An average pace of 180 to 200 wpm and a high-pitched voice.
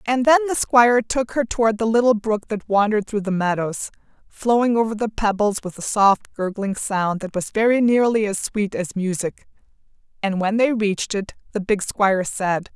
Yes: average, 195 wpm; high, 215 Hz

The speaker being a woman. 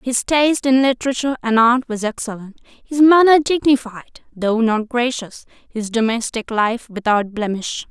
Yes: female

